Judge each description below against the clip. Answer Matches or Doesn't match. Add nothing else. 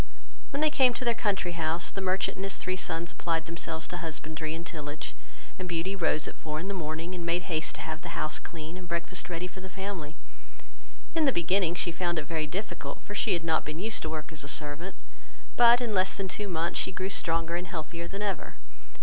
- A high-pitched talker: Doesn't match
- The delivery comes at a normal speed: Doesn't match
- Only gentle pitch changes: Doesn't match